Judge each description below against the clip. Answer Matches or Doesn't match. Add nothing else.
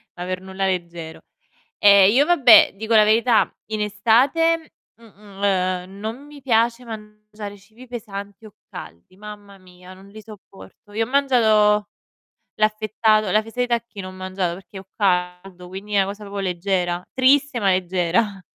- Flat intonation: Doesn't match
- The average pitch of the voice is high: Matches